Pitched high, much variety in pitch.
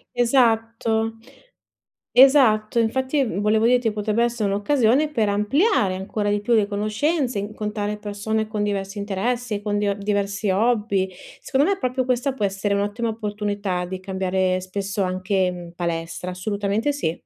No: high, 210 Hz; average, 2.8 semitones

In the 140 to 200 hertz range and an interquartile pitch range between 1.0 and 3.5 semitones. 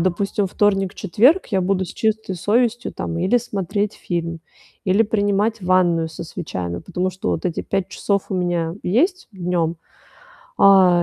Yes: high, 190 Hz; average, 3.0 semitones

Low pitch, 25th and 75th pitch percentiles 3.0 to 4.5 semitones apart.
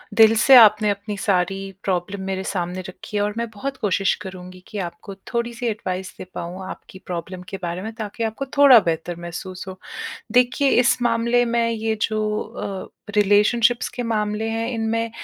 No: high, 210 Hz; average, 3.4 semitones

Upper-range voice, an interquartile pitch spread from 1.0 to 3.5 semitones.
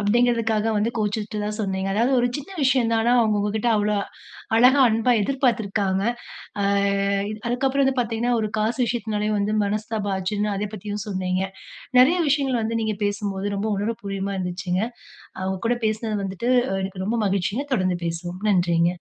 Yes: high, 210 Hz; average, 2.9 semitones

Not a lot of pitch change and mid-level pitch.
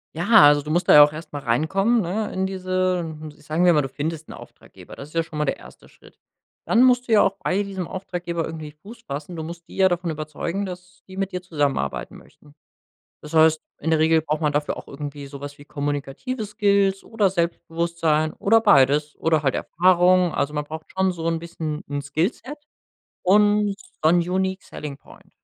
No: average, 3.8 semitones; medium, 165 Hz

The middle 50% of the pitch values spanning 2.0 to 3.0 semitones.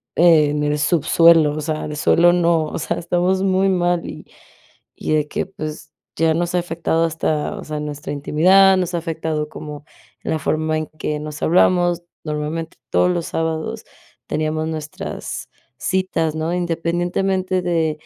Yes: narrow, 2.4 semitones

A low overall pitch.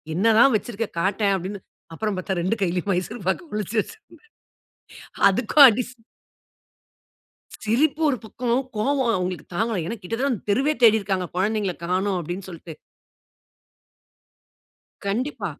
No: high, 210 Hz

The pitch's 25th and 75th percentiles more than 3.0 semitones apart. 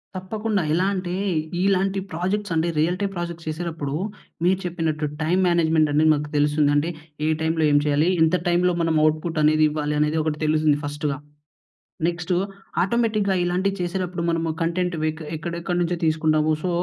No: average, 2.7 semitones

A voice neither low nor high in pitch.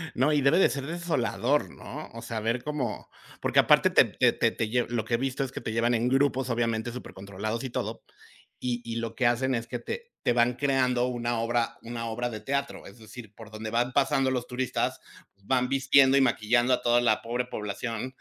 No: low, 120 Hz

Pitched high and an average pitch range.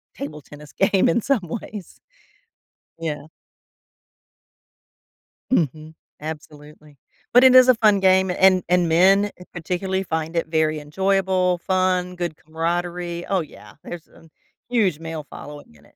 No: medium, 175 Hz; average, 3.4 semitones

